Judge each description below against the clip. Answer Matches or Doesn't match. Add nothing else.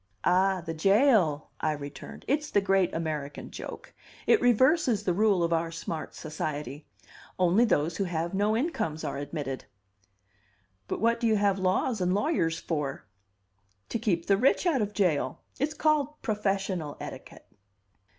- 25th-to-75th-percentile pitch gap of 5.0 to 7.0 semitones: Matches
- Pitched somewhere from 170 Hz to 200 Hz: Matches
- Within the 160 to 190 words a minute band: Doesn't match